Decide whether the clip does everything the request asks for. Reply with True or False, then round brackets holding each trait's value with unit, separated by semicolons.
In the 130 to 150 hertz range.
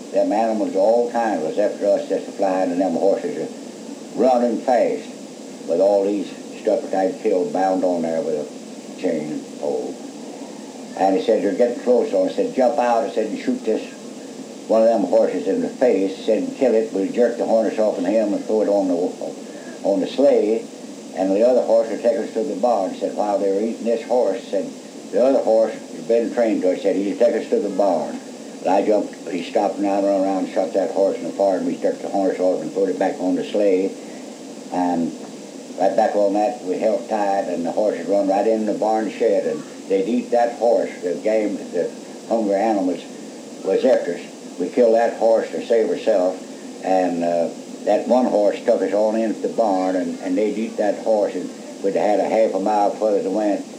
False (110 Hz)